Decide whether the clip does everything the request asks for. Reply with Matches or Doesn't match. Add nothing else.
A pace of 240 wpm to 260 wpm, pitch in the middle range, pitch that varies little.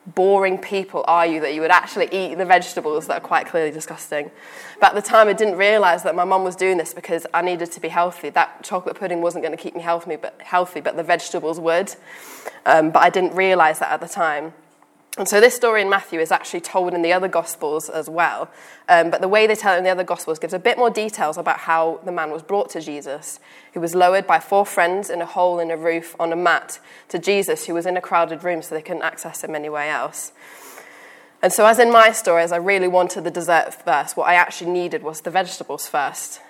Matches